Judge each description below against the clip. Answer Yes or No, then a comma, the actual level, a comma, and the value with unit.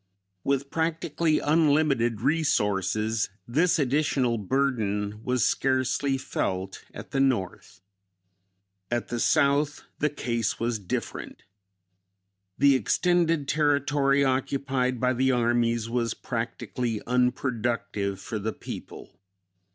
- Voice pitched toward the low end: Yes, low, 125 Hz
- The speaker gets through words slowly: Yes, slow, 100 wpm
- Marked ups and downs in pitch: No, average, 3.6 semitones